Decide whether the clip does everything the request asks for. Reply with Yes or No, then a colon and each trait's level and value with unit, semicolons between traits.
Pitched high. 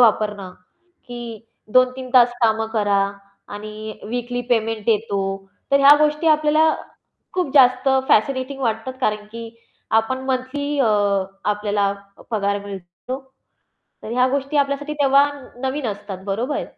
Yes: high, 245 Hz